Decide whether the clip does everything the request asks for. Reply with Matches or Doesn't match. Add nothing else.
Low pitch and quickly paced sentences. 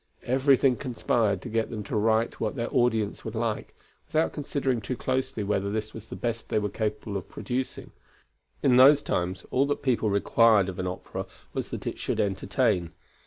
Doesn't match